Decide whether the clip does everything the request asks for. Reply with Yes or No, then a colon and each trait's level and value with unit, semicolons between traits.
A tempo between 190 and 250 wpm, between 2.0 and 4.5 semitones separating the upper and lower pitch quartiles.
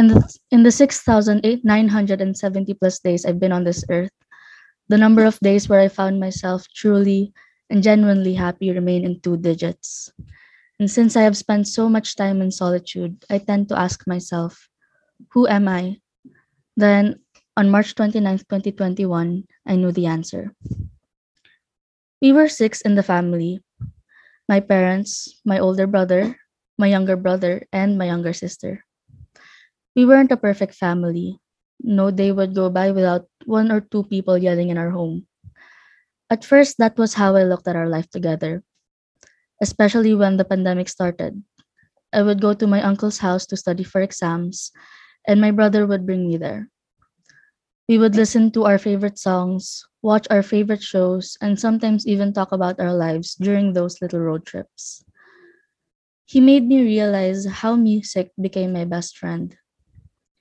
No: average, 155 wpm; average, 2.9 semitones